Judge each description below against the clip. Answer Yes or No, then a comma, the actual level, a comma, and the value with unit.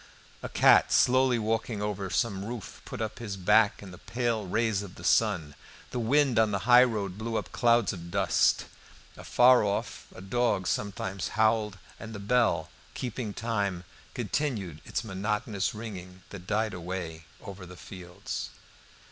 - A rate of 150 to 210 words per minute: Yes, average, 155 wpm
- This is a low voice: Yes, low, 105 Hz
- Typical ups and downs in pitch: Yes, average, 3.5 semitones